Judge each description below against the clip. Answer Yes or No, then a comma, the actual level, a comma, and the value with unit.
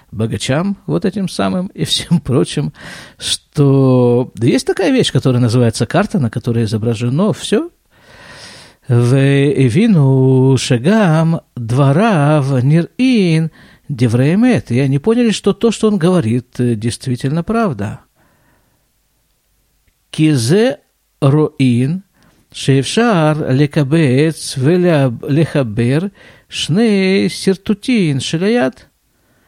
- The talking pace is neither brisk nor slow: No, slow, 90 wpm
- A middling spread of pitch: No, wide, 7.0 semitones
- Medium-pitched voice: Yes, medium, 150 Hz